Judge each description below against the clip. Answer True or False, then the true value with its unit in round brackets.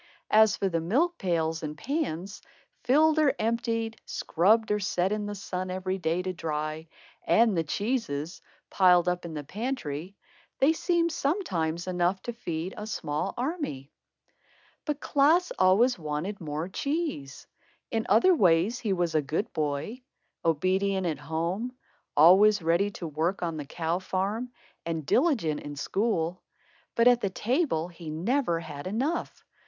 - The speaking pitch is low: False (185 Hz)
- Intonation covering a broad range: True (6.1 semitones)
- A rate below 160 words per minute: True (150 wpm)